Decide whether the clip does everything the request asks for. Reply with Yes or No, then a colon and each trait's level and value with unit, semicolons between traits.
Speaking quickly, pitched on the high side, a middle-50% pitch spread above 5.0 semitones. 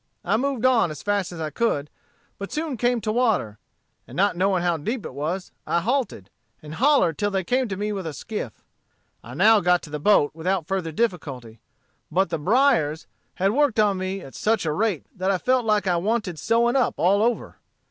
Yes: fast, 210 wpm; high, 195 Hz; wide, 5.5 semitones